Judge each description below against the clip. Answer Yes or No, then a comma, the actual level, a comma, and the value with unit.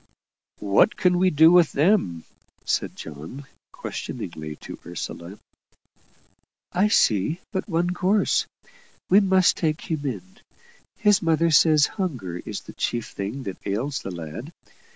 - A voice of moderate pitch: Yes, medium, 155 Hz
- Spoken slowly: Yes, slow, 130 wpm